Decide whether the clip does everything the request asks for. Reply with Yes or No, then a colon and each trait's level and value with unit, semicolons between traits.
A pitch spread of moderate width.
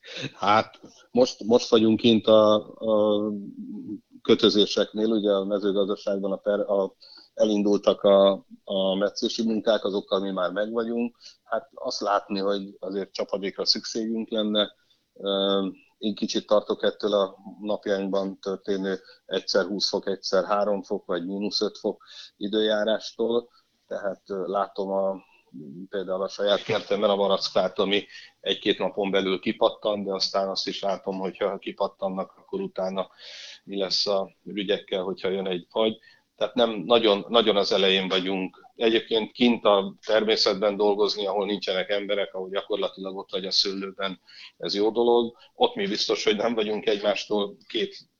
No: narrow, 2.3 semitones